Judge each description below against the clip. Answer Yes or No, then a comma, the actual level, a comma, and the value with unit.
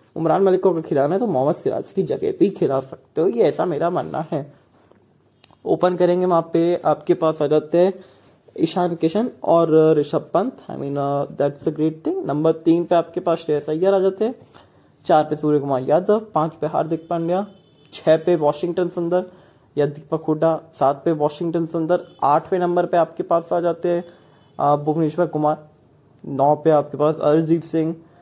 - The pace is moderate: Yes, average, 175 wpm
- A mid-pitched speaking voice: Yes, medium, 165 Hz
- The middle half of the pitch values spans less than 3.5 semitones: Yes, average, 2.7 semitones